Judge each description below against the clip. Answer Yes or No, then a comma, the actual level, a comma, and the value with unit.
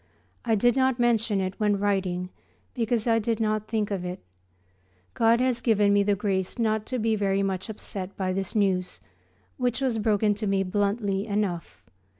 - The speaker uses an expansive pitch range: No, average, 2.7 semitones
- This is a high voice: Yes, high, 210 Hz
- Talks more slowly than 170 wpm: No, average, 175 wpm